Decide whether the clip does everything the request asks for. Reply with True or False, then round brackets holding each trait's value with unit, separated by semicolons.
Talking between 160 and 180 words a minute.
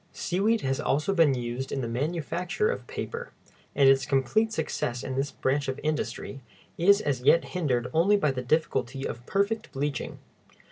True (170 wpm)